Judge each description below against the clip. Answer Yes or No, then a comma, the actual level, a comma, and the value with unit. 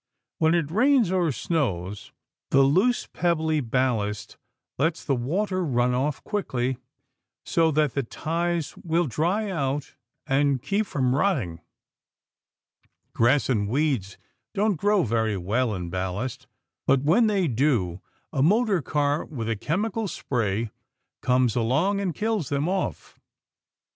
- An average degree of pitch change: No, wide, 6.4 semitones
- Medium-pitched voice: Yes, medium, 145 Hz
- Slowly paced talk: Yes, slow, 130 wpm